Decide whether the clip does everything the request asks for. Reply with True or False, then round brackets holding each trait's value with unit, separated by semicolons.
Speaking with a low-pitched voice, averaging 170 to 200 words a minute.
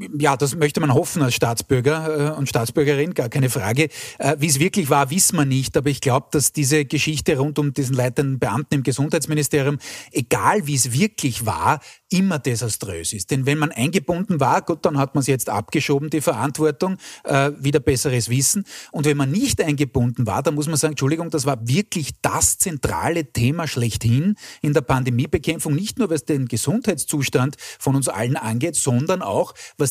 False (145 Hz; 180 wpm)